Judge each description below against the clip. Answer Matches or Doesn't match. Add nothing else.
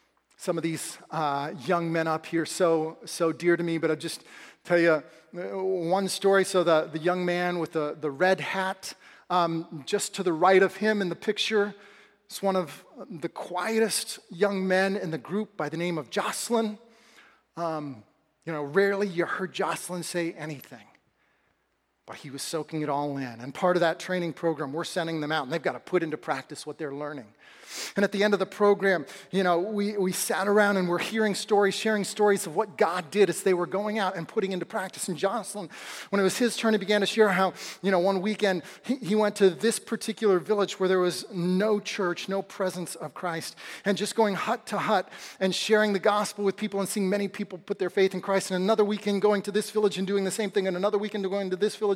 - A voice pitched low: Doesn't match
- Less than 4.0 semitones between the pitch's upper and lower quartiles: Matches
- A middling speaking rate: Doesn't match